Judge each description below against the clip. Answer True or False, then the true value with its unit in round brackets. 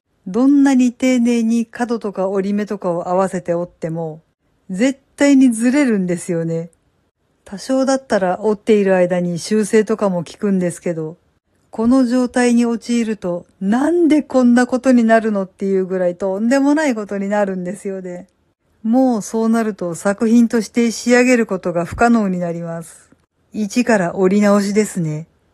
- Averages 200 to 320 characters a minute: False (330 characters per minute)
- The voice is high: True (210 Hz)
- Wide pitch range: False (4.9 semitones)